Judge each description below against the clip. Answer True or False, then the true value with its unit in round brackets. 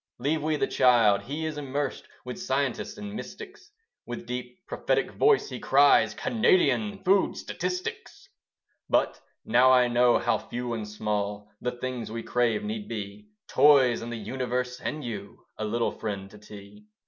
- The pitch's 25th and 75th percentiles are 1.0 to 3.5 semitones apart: False (5.3 semitones)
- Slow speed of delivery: False (160 wpm)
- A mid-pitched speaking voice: False (125 Hz)